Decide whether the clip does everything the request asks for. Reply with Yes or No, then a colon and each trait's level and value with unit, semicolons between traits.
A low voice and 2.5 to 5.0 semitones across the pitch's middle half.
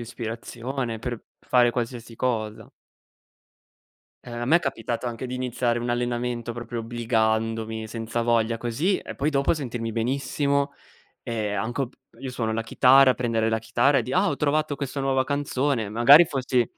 Yes: low, 120 Hz; average, 2.8 semitones